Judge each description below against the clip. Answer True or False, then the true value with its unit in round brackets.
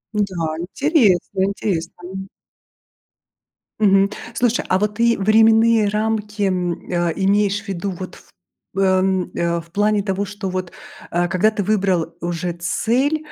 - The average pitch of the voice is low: False (195 Hz)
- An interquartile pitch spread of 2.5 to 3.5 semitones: True (2.9 semitones)